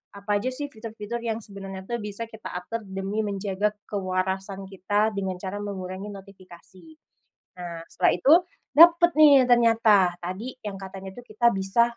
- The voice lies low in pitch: No, high, 205 Hz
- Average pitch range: Yes, average, 3.1 semitones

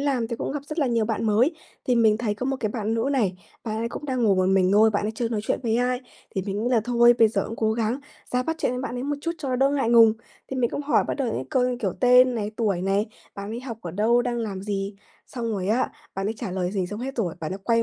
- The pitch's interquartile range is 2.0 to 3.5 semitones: Yes, average, 3.2 semitones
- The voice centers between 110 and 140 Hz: No, high, 230 Hz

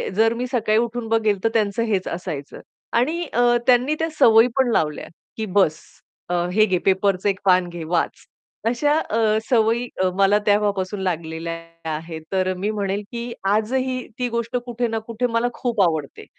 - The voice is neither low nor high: No, high, 215 Hz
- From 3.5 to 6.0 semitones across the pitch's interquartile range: Yes, average, 4.1 semitones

